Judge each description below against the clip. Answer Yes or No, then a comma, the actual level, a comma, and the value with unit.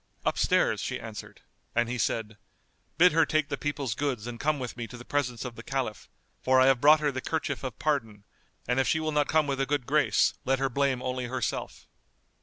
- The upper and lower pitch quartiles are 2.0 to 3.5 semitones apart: Yes, average, 3.1 semitones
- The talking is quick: Yes, fast, 220 wpm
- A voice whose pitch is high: No, low, 135 Hz